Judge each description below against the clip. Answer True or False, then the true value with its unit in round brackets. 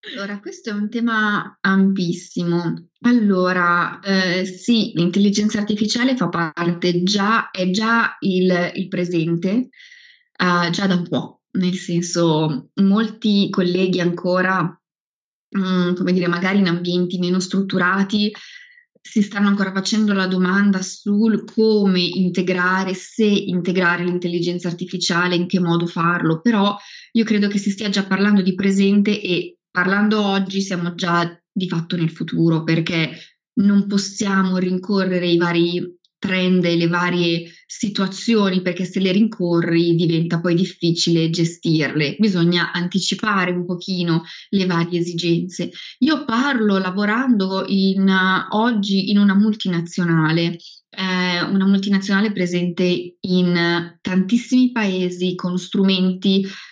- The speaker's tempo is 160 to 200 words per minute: False (125 wpm)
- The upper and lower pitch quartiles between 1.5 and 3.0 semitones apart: True (2.5 semitones)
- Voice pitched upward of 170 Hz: True (185 Hz)